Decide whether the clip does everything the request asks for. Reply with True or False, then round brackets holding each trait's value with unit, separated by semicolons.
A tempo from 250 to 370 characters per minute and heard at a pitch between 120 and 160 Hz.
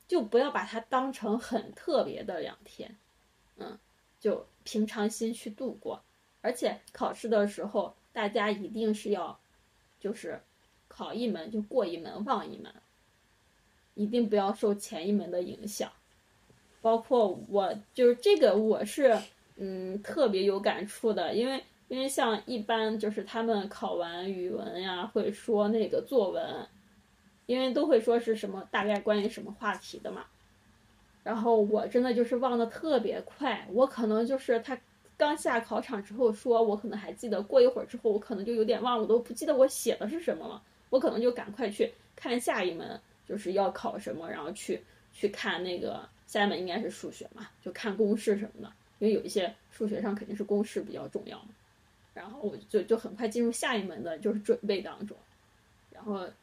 False (265 characters per minute; 220 Hz)